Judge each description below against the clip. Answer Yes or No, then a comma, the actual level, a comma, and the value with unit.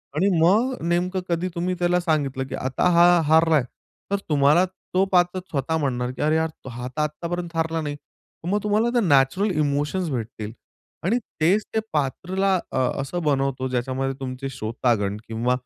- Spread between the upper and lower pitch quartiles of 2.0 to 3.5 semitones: No, average, 5.0 semitones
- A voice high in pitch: No, medium, 155 Hz